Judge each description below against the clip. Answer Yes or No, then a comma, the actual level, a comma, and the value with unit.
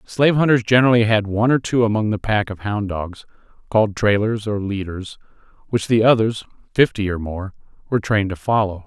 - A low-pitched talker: Yes, low, 105 Hz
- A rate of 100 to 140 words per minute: No, average, 185 wpm